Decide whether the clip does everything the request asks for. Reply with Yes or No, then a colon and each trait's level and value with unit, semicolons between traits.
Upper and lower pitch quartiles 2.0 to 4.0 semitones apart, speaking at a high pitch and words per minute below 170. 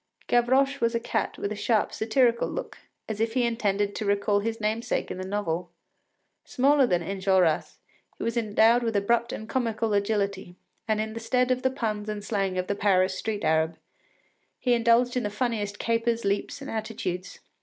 No: average, 2.7 semitones; high, 220 Hz; average, 185 wpm